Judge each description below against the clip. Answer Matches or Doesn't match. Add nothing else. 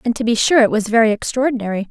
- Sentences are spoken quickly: Matches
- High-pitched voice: Matches